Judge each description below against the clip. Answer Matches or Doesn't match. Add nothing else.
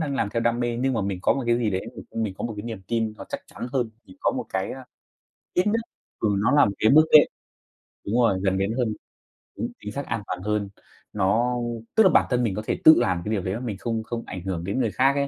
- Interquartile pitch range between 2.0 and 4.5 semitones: Matches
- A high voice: Doesn't match